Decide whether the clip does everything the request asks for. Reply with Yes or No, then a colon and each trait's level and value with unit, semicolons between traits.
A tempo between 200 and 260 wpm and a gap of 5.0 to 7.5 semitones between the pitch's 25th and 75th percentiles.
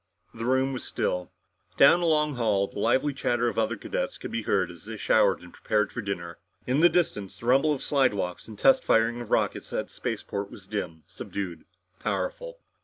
Yes: fast, 205 wpm; wide, 5.5 semitones